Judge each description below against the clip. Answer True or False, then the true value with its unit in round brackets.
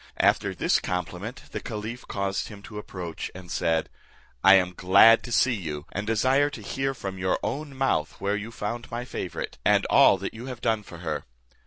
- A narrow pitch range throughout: False (4.5 semitones)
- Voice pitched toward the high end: False (105 Hz)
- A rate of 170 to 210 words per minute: True (195 wpm)